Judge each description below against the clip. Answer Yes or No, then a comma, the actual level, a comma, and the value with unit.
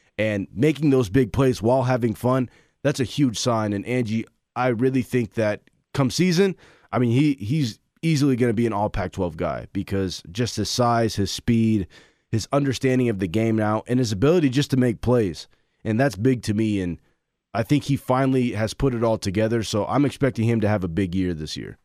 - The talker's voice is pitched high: No, low, 120 Hz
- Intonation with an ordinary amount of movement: Yes, average, 3.8 semitones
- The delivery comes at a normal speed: No, fast, 215 wpm